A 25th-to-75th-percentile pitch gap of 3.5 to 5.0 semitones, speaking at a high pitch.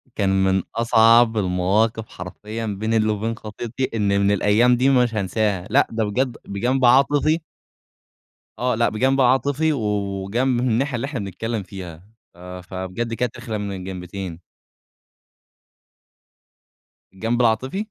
No: average, 4.0 semitones; low, 110 Hz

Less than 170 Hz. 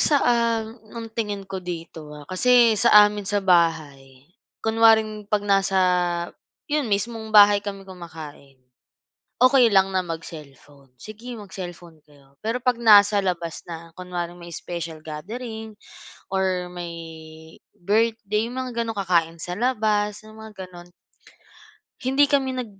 No: high, 195 Hz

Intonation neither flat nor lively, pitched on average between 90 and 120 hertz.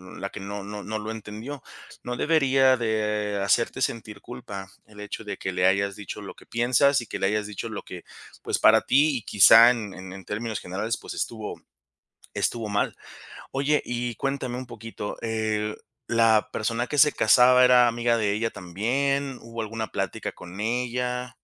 Yes: average, 3.0 semitones; low, 115 Hz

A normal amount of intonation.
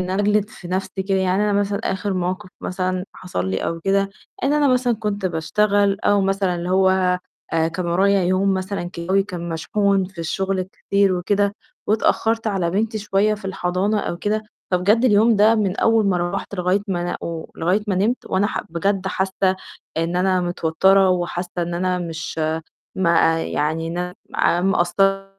No: narrow, 2.3 semitones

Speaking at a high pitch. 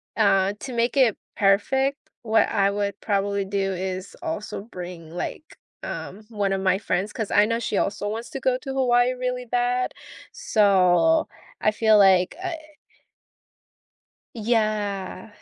Yes: high, 210 Hz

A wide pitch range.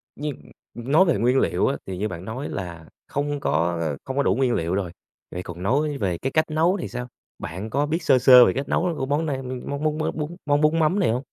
Yes: wide, 7.2 semitones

